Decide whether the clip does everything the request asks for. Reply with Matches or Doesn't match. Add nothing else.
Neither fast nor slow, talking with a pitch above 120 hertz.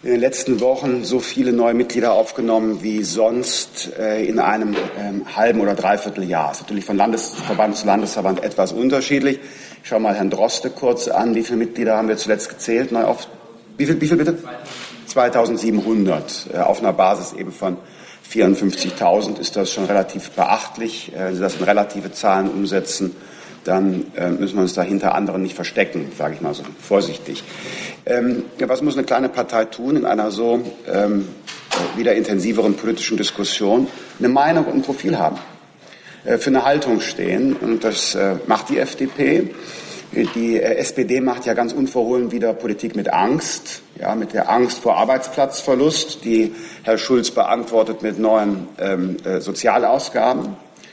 Doesn't match